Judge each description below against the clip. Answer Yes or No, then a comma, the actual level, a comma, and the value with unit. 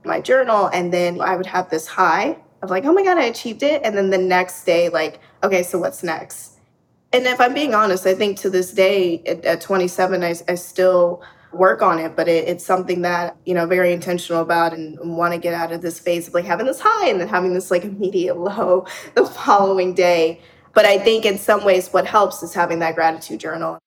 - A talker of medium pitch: Yes, medium, 180 Hz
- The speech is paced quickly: Yes, fast, 230 wpm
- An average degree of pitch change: No, narrow, 2.2 semitones